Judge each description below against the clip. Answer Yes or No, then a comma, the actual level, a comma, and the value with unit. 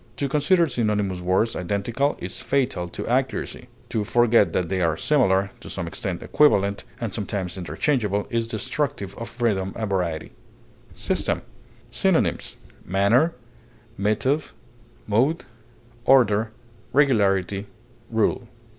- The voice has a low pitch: Yes, low, 110 Hz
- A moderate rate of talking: No, slow, 115 wpm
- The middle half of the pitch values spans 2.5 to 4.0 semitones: No, average, 4.9 semitones